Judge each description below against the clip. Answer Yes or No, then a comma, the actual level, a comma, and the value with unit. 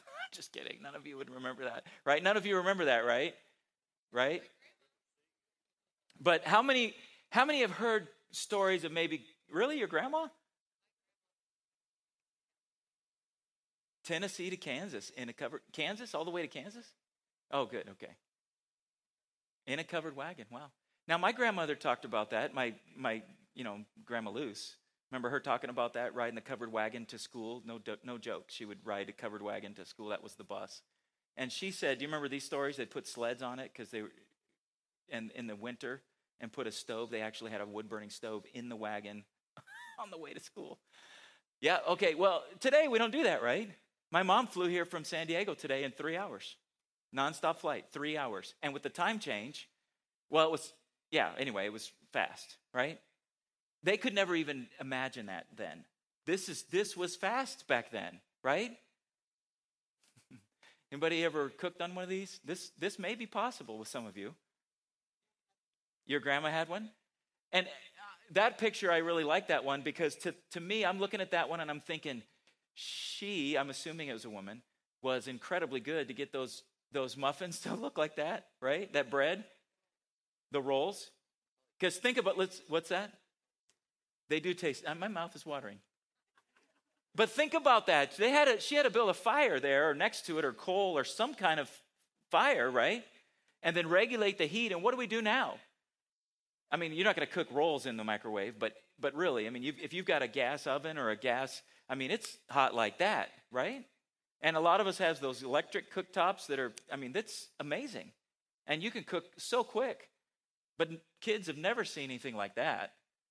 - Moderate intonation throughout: No, wide, 6.5 semitones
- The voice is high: No, medium, 160 Hz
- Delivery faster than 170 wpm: Yes, average, 185 wpm